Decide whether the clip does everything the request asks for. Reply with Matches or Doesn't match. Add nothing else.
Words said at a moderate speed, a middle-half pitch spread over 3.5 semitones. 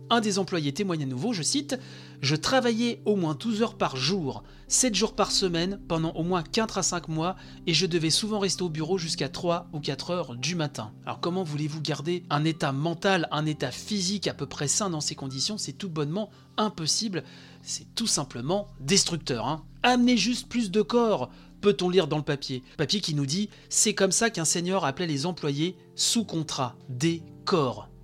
Matches